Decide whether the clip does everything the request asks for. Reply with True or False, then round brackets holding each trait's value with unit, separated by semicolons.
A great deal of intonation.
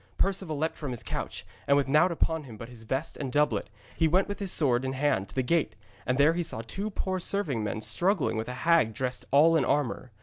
False (5.0 semitones)